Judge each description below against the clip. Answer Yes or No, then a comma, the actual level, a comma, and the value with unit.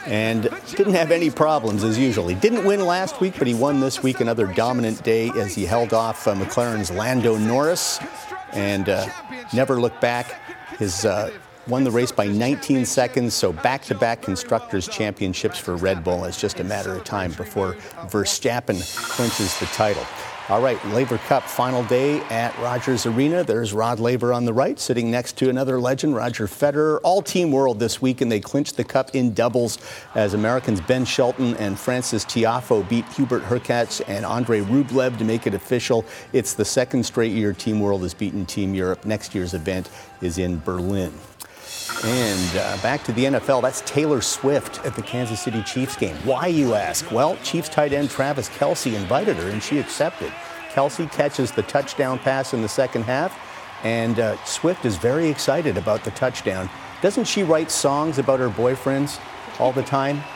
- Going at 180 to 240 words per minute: Yes, average, 185 wpm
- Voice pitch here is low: Yes, low, 120 Hz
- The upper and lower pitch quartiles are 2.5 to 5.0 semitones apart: Yes, average, 3.9 semitones